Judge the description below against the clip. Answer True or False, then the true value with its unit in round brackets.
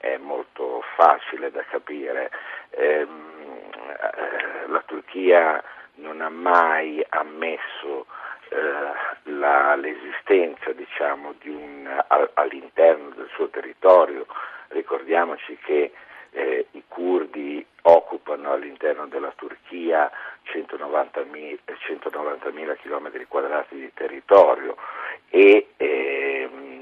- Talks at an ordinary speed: False (85 wpm)